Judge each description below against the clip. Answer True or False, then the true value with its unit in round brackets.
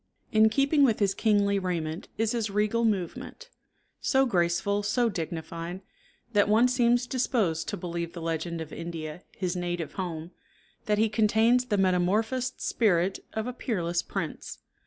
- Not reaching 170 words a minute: True (150 wpm)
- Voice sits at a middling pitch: False (200 Hz)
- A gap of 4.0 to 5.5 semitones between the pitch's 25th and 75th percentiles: True (4.8 semitones)